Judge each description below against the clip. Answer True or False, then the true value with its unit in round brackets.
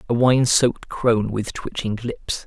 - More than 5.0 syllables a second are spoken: False (4.5 syllables/s)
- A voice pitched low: True (115 Hz)